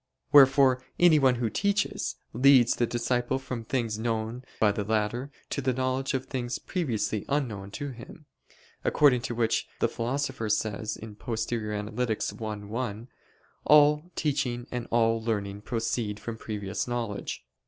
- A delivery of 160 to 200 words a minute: No, slow, 135 wpm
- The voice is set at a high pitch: No, low, 120 Hz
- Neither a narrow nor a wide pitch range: Yes, average, 3.4 semitones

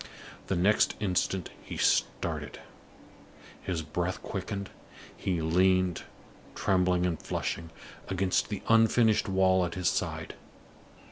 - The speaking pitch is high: No, very low, 95 Hz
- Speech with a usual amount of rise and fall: No, narrow, 1.6 semitones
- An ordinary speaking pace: No, slow, 110 wpm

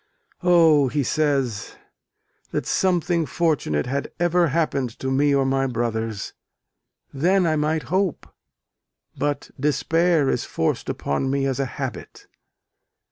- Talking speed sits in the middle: No, slow, 125 wpm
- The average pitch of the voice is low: No, medium, 145 Hz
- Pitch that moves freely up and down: No, average, 3.9 semitones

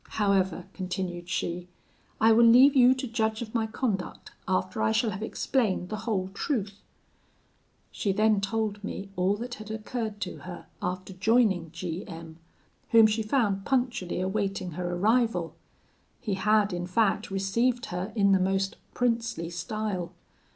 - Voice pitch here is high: Yes, high, 200 Hz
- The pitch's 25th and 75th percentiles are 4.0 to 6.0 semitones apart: No, average, 3.5 semitones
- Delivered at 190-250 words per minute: No, average, 150 wpm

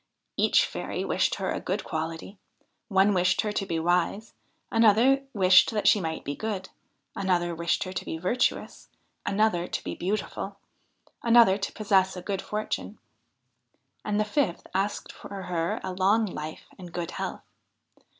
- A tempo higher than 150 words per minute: Yes, average, 160 wpm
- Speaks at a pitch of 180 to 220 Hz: Yes, high, 190 Hz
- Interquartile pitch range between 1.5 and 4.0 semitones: Yes, average, 3.2 semitones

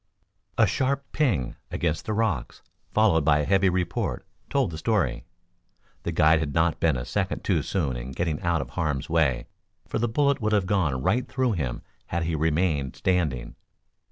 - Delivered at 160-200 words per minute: Yes, average, 180 wpm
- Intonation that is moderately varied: No, wide, 6.0 semitones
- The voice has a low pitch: Yes, very low, 85 Hz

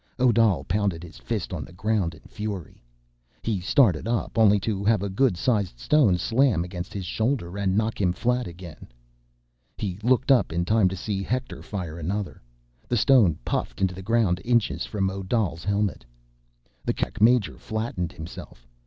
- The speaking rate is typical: Yes, average, 170 wpm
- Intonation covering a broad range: No, average, 4.1 semitones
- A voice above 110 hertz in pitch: No, low, 100 Hz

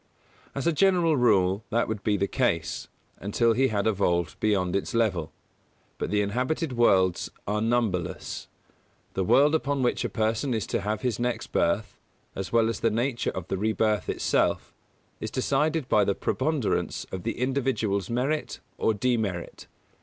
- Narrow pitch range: No, average, 4.4 semitones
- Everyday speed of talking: Yes, average, 160 wpm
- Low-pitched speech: Yes, low, 110 Hz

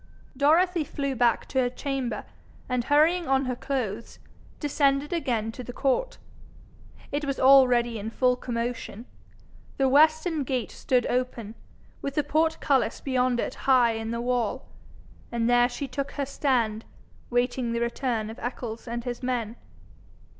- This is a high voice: Yes, very high, 255 Hz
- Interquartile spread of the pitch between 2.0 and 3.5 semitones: Yes, average, 2.7 semitones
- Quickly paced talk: No, average, 145 wpm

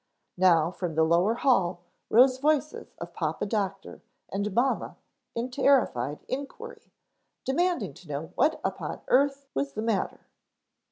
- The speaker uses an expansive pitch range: Yes, wide, 7.7 semitones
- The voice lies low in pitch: No, high, 225 Hz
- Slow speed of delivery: Yes, slow, 130 wpm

